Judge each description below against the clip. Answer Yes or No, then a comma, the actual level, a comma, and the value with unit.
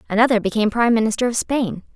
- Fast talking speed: No, average, 185 wpm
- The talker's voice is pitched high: Yes, high, 225 Hz